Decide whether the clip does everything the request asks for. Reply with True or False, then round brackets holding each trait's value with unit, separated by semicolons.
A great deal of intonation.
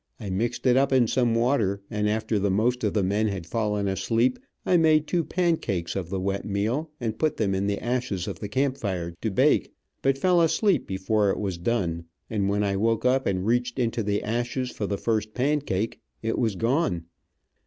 False (4.2 semitones)